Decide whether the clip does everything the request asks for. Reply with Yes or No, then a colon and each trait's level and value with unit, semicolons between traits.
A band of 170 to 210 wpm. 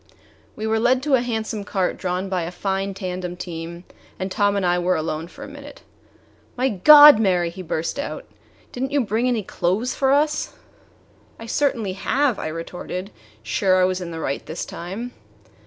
Yes: average, 185 wpm